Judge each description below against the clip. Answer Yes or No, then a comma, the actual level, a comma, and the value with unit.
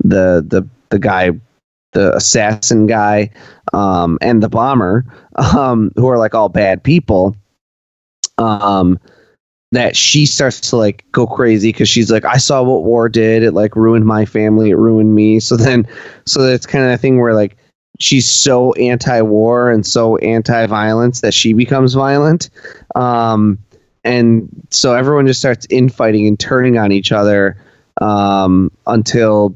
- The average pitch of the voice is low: Yes, low, 115 Hz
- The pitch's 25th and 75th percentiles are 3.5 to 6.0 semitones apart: No, average, 3.0 semitones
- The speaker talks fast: No, average, 160 wpm